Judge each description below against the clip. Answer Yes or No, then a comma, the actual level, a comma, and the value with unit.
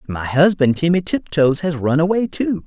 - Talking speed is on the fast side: No, average, 180 wpm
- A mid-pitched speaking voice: Yes, medium, 160 Hz